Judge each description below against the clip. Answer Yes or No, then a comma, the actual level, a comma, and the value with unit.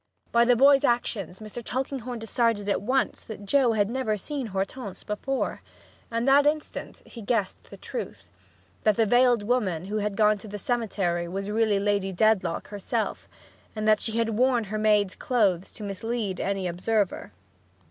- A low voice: No, high, 215 Hz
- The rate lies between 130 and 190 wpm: Yes, average, 170 wpm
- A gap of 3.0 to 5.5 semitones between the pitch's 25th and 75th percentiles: Yes, average, 3.3 semitones